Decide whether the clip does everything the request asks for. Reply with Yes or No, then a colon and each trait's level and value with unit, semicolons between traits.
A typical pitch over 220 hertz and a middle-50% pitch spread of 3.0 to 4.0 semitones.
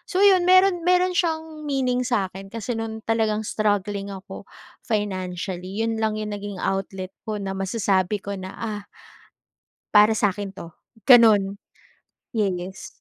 No: high, 210 Hz; average, 3.7 semitones